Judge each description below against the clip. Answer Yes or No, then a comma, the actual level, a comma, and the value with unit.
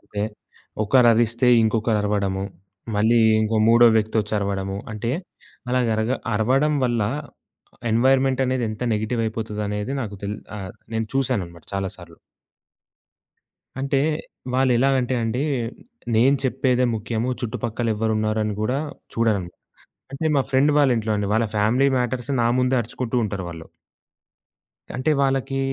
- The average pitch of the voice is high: No, low, 115 Hz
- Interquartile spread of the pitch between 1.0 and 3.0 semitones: No, average, 3.4 semitones